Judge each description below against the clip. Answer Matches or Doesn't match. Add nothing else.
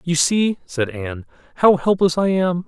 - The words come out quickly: Doesn't match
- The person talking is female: Doesn't match